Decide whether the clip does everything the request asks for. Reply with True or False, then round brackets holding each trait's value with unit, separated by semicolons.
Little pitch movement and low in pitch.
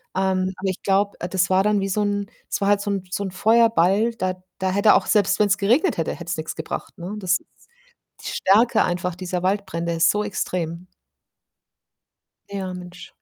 False (1.9 semitones; 190 Hz)